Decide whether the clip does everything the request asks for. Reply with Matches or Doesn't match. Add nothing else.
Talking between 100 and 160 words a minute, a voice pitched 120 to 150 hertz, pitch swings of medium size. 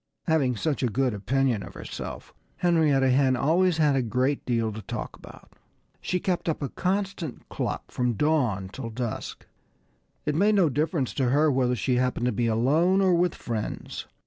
Doesn't match